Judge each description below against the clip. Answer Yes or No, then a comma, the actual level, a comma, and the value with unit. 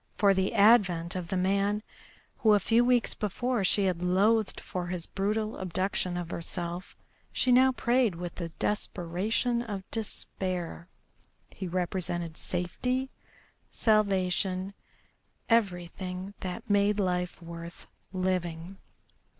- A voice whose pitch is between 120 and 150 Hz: No, high, 190 Hz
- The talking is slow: Yes, slow, 120 wpm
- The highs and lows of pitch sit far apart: No, average, 3.2 semitones